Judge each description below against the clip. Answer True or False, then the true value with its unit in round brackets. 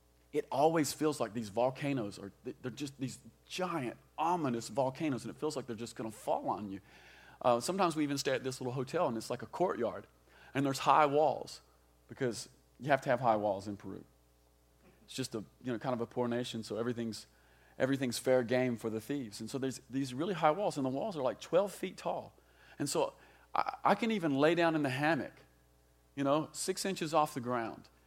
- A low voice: True (125 Hz)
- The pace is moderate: False (215 wpm)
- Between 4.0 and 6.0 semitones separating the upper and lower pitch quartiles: True (5.3 semitones)